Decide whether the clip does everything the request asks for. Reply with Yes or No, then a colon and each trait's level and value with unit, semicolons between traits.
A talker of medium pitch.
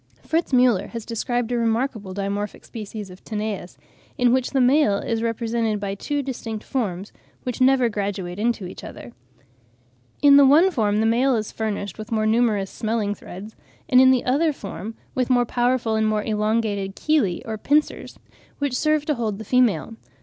No: high, 225 Hz